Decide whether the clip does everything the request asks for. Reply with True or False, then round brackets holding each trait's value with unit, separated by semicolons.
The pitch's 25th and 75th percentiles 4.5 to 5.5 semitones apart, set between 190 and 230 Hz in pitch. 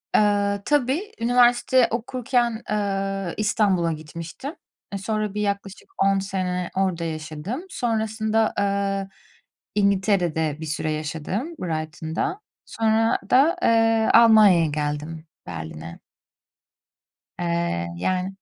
True (5.2 semitones; 200 Hz)